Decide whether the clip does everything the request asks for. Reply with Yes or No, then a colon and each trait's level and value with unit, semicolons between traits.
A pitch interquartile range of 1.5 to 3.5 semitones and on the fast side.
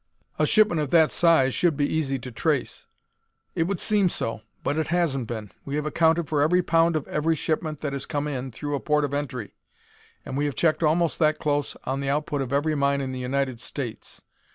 Yes: average, 2.8 semitones; fast, 220 wpm